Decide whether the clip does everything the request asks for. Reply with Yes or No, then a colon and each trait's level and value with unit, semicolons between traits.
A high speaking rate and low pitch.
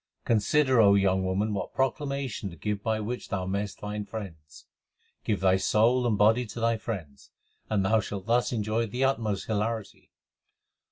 No: average, 165 wpm; low, 105 Hz